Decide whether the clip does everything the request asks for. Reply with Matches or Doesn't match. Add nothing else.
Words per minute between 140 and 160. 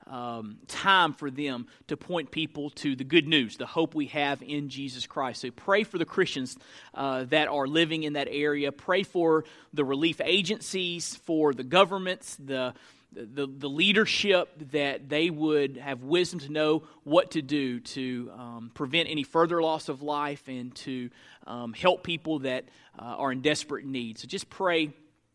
Doesn't match